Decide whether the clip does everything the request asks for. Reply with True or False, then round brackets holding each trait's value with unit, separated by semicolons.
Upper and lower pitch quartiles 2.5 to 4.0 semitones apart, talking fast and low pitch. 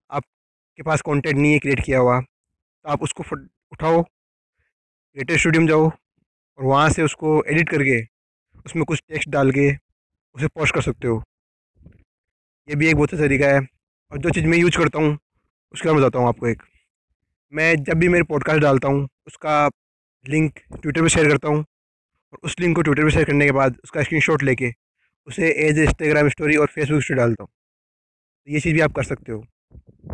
False (2.9 semitones; 195 wpm; 150 Hz)